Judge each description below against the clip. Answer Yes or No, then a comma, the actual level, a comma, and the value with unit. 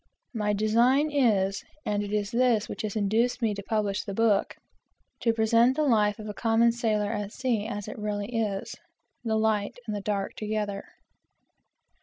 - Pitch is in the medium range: No, high, 215 Hz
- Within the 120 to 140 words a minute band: No, average, 175 wpm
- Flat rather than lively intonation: Yes, narrow, 2.0 semitones